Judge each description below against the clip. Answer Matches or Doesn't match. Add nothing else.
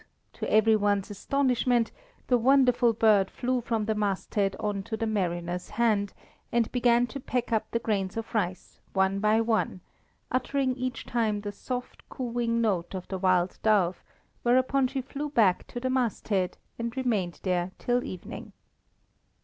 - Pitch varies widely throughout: Doesn't match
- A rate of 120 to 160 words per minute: Matches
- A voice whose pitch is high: Matches